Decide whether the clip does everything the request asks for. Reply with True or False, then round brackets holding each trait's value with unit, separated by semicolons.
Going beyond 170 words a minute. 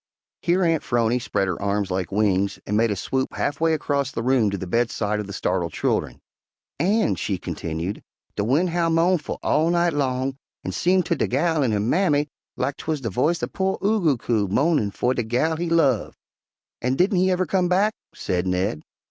True (205 wpm)